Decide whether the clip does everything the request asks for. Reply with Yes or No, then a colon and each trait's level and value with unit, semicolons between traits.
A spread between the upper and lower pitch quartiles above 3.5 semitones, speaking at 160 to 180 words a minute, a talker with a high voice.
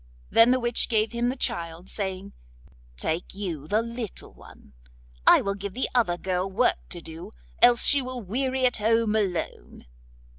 Yes: average, 4.7 semitones; average, 165 wpm; high, 210 Hz